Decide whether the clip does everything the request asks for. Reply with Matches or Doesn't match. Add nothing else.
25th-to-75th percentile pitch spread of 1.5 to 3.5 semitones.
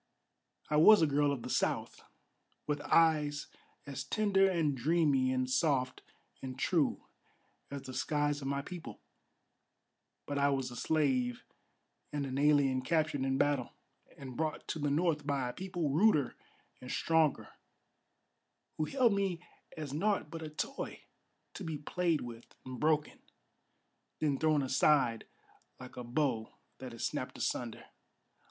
Matches